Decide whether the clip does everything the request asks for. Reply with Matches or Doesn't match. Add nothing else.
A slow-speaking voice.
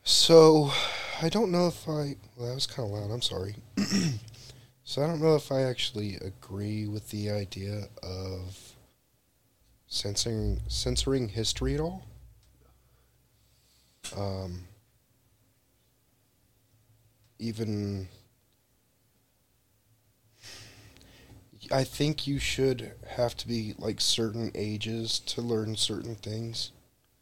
Matches